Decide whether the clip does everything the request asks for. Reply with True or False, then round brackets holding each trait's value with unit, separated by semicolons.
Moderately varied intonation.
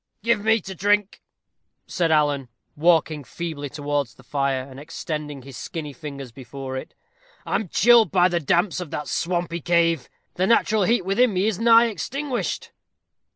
False (6.0 semitones)